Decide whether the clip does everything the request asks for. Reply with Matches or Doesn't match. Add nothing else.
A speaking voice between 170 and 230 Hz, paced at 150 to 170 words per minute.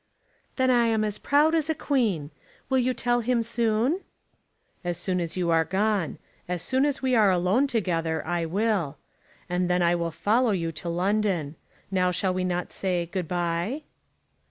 Doesn't match